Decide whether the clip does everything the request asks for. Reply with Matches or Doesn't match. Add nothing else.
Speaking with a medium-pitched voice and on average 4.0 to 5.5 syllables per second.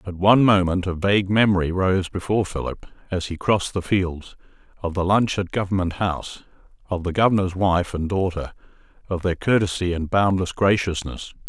Doesn't match